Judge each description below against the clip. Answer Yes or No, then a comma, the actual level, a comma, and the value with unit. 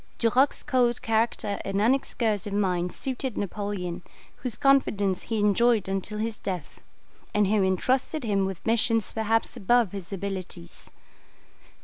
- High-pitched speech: Yes, high, 210 Hz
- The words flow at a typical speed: No, slow, 125 wpm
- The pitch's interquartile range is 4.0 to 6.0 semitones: No, average, 3.3 semitones